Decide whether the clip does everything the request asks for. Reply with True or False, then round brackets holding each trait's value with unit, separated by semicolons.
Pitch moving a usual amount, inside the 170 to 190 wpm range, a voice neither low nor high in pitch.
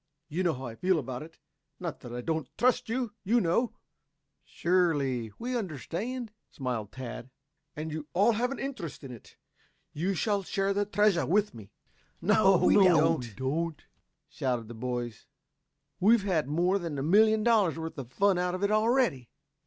False (7.5 semitones; 175 wpm; 175 Hz)